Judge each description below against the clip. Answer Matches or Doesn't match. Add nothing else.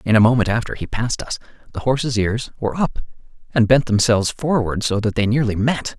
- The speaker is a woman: Doesn't match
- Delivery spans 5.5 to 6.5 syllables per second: Matches